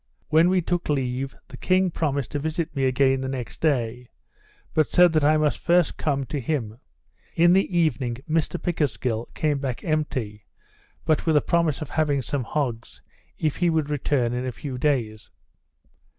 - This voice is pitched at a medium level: Yes, medium, 145 Hz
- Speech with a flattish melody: No, average, 3.8 semitones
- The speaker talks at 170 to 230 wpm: Yes, average, 175 wpm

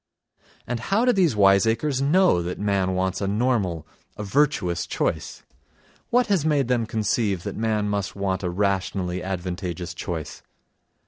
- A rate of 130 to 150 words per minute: Yes, average, 145 wpm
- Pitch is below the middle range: Yes, low, 100 Hz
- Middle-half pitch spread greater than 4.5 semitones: Yes, average, 5.2 semitones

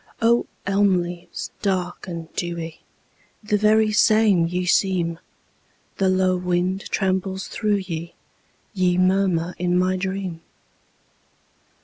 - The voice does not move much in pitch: Yes, narrow, 1.9 semitones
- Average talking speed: No, slow, 110 wpm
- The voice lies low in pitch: No, medium, 185 Hz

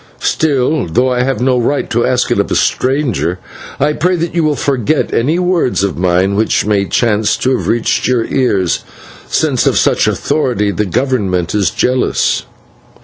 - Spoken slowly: No, average, 175 wpm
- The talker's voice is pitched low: Yes, low, 125 Hz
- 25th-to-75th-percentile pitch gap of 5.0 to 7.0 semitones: Yes, average, 5.3 semitones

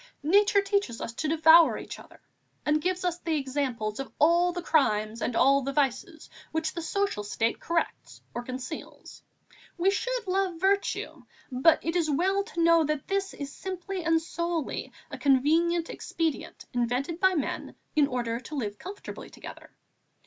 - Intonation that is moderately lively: Yes, average, 4.7 semitones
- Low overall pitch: No, very high, 320 Hz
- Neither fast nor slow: Yes, average, 165 wpm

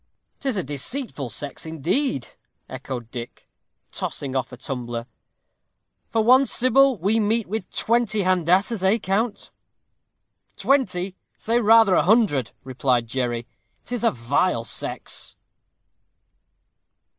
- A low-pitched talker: No, medium, 185 Hz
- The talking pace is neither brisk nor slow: No, slow, 110 wpm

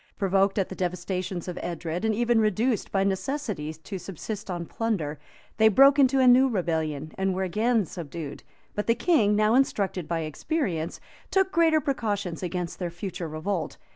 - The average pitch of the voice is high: Yes, high, 195 Hz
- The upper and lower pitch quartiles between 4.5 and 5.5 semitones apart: Yes, average, 5.0 semitones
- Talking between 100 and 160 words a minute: No, average, 170 wpm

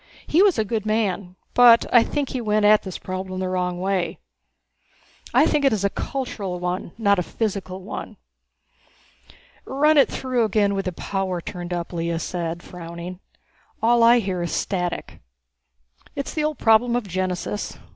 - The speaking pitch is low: No, high, 200 Hz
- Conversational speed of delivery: Yes, average, 165 wpm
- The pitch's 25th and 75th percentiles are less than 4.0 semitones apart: No, average, 4.5 semitones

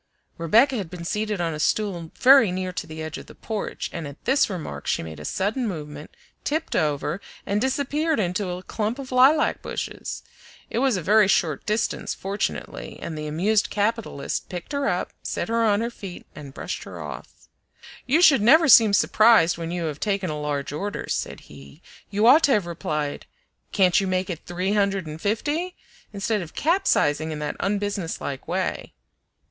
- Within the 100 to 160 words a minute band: No, average, 185 wpm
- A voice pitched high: Yes, high, 200 Hz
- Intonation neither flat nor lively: No, wide, 5.8 semitones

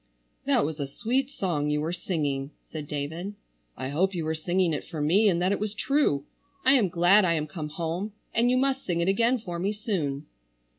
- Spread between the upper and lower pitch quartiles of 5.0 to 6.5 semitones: Yes, average, 5.3 semitones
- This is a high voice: No, medium, 175 Hz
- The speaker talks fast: Yes, fast, 215 wpm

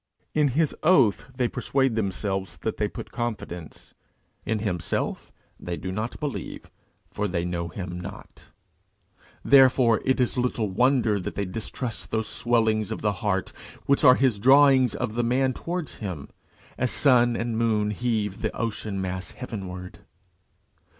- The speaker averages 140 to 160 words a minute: Yes, average, 150 wpm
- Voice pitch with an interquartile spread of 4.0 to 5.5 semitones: Yes, average, 4.6 semitones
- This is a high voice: No, low, 110 Hz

